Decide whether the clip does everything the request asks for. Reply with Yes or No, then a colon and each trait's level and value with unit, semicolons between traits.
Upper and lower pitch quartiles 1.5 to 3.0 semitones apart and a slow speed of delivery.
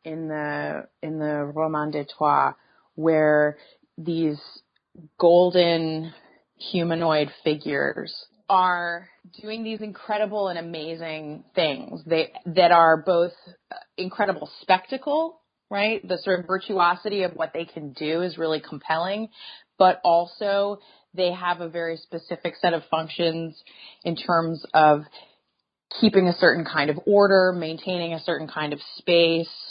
Yes: average, 2.7 semitones; slow, 125 wpm